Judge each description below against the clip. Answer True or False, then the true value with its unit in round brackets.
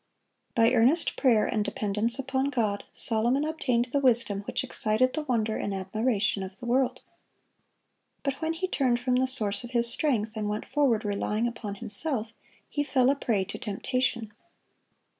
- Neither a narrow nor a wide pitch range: True (3.5 semitones)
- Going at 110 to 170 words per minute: True (165 wpm)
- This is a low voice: False (235 Hz)